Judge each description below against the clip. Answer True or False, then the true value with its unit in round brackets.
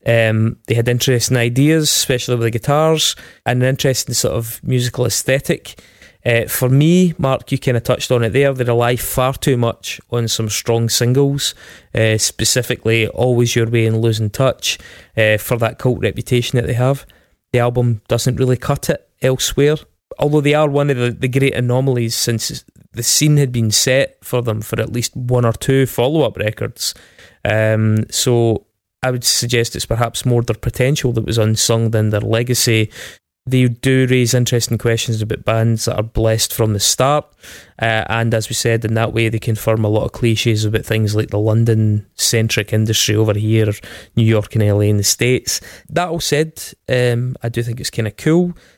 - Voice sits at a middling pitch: False (120 Hz)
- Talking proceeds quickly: False (190 wpm)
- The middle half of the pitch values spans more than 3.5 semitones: False (2.5 semitones)